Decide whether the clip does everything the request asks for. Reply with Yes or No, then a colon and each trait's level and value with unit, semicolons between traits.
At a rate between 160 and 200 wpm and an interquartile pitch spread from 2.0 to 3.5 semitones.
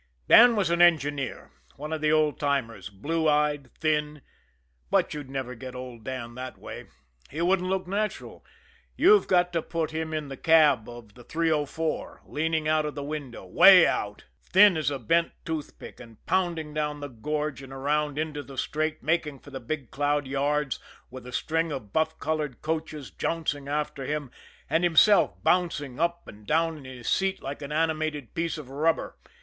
Yes: average, 180 wpm; average, 2.9 semitones